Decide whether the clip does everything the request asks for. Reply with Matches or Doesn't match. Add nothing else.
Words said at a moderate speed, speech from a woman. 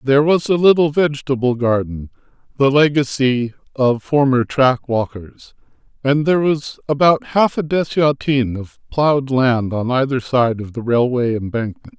Doesn't match